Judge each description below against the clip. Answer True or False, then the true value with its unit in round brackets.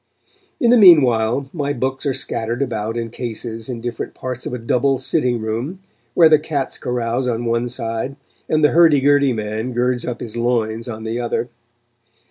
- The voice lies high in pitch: False (125 Hz)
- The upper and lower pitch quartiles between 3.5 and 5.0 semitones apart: False (3.1 semitones)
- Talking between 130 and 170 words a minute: False (180 wpm)